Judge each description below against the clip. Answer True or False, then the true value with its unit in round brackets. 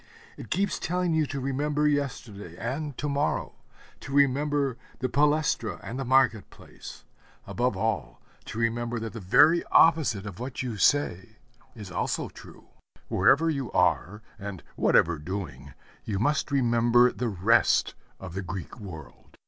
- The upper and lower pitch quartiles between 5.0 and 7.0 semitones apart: True (5.6 semitones)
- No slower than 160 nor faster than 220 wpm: False (150 wpm)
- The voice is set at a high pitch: False (120 Hz)